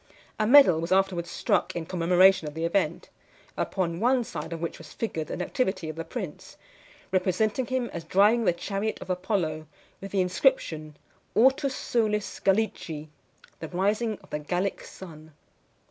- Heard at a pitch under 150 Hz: No, medium, 185 Hz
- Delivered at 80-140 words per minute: No, average, 160 wpm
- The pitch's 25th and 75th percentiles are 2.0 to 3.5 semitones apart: No, average, 4.6 semitones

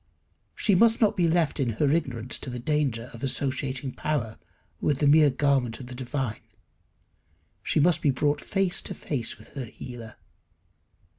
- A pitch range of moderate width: Yes, average, 3.9 semitones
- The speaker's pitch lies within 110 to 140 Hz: Yes, low, 135 Hz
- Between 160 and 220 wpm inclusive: Yes, average, 165 wpm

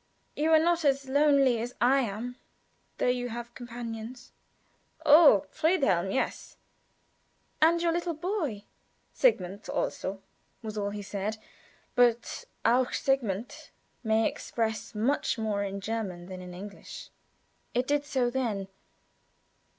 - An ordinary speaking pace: No, slow, 125 wpm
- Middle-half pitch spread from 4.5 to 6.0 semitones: Yes, average, 4.9 semitones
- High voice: Yes, high, 240 Hz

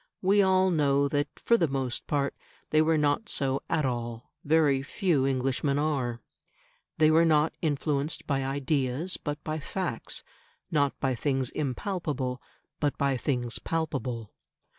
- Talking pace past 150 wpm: No, average, 140 wpm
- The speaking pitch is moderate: Yes, medium, 145 Hz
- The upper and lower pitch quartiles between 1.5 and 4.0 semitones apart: Yes, average, 2.9 semitones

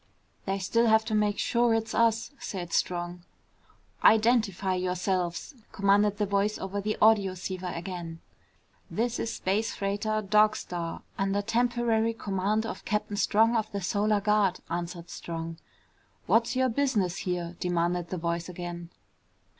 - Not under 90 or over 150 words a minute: Yes, average, 140 wpm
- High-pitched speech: Yes, high, 200 Hz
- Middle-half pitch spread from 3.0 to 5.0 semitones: Yes, average, 3.5 semitones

